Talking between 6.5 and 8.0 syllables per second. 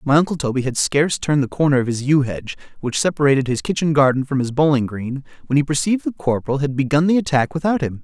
Yes: 6.8 syllables/s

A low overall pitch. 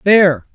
No: medium, 170 Hz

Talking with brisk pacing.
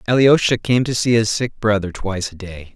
Yes: fast, 215 wpm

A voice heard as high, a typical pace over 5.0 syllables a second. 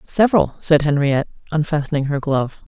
No: medium, 150 Hz; 6.1 syllables/s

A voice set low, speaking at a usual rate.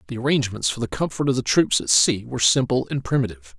No: low, 120 Hz; fast, 235 wpm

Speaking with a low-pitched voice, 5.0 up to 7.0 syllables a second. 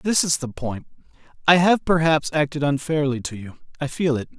No: medium, 150 Hz; 5.3 syllables/s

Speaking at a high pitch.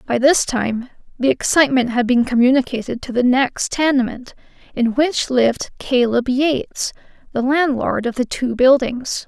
Yes: very high, 255 Hz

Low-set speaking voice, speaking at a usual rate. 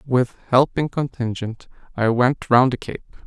Yes: low, 125 Hz; average, 145 wpm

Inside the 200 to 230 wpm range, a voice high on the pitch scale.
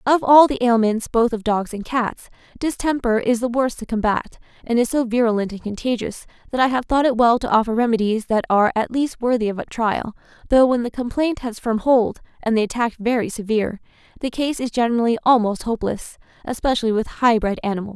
Yes: fast, 205 wpm; high, 235 Hz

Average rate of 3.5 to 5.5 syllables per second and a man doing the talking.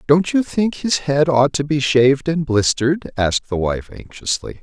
Yes: 4.8 syllables/s; male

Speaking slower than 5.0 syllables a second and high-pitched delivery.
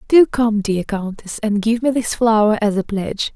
Yes: 4.8 syllables/s; high, 220 Hz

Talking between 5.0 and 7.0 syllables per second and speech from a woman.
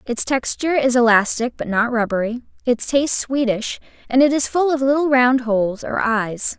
Yes: 5.1 syllables/s; female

